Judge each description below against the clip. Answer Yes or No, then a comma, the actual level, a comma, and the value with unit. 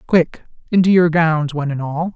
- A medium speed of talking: Yes, average, 195 wpm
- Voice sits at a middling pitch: Yes, medium, 165 Hz